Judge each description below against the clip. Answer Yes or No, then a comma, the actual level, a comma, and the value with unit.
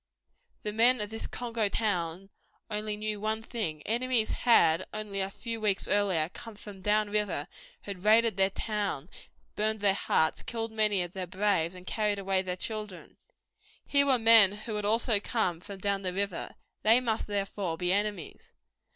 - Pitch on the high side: Yes, high, 205 Hz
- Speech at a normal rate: Yes, average, 170 wpm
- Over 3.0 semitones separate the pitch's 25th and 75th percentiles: No, narrow, 2.4 semitones